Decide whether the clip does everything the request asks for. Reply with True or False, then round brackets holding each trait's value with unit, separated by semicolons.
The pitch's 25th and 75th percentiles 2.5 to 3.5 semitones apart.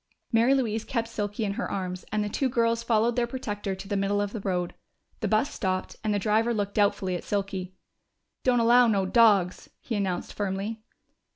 True (2.8 semitones)